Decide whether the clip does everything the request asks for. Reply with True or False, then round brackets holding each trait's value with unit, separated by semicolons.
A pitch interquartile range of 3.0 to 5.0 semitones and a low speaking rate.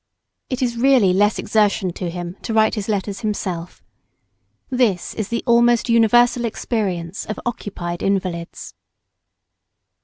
True (4.3 semitones; 125 wpm)